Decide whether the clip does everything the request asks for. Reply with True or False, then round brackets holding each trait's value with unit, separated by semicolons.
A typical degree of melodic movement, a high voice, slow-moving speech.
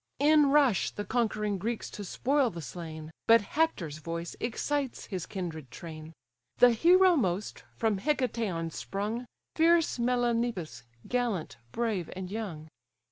False (6.3 semitones; 220 Hz; 130 wpm)